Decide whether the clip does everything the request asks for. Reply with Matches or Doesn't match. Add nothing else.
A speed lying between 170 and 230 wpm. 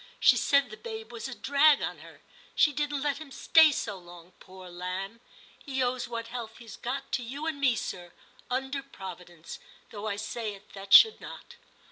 Matches